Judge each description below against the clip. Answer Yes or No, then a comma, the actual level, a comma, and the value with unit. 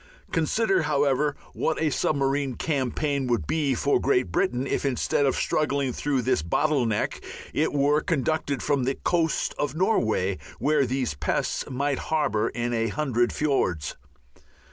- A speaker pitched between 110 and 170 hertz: Yes, medium, 140 Hz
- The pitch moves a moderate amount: Yes, average, 3.4 semitones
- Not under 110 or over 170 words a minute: Yes, average, 145 wpm